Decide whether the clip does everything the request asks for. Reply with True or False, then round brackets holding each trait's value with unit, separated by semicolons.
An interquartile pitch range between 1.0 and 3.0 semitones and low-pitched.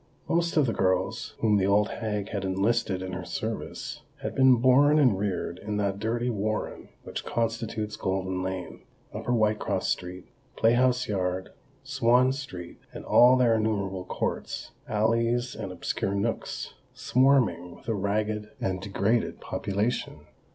False (3.9 semitones; 105 Hz)